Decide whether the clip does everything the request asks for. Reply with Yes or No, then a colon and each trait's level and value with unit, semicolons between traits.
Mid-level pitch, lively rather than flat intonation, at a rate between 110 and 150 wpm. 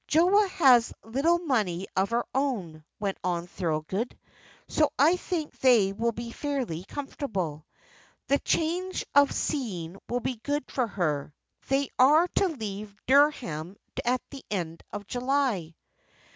No: high, 240 Hz; wide, 7.1 semitones; average, 140 wpm